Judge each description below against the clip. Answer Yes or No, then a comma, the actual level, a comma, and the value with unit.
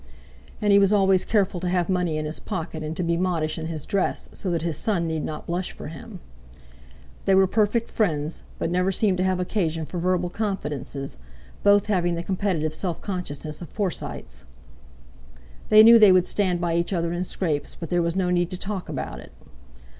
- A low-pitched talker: No, medium, 180 Hz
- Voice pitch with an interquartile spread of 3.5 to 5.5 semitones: No, average, 2.9 semitones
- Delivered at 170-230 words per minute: Yes, average, 200 wpm